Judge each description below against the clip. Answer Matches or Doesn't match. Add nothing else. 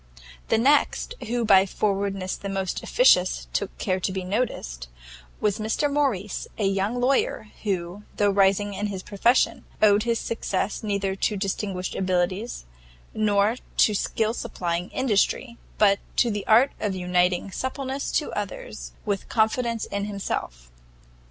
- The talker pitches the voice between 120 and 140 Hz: Doesn't match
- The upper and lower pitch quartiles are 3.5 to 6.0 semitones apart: Doesn't match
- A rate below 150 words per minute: Matches